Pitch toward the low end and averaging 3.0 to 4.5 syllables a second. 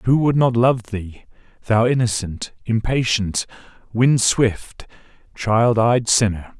Yes: low, 115 Hz; 3.5 syllables/s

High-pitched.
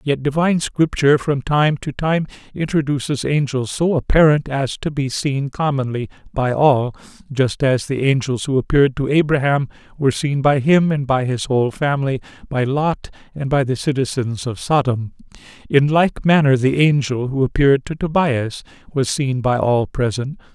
No: low, 135 Hz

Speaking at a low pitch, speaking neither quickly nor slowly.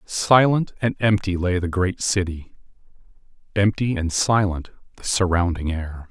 No: very low, 95 Hz; slow, 120 wpm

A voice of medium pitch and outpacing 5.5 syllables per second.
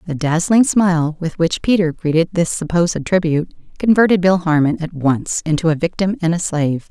No: medium, 170 Hz; 5.3 syllables/s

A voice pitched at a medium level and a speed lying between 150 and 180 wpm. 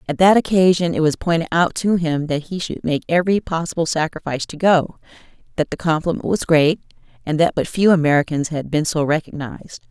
No: medium, 165 Hz; average, 195 wpm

